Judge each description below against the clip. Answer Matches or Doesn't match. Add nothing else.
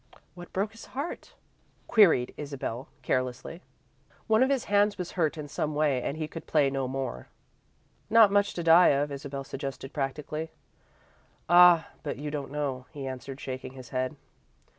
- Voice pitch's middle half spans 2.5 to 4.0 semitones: Doesn't match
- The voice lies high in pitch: Doesn't match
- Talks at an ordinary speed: Matches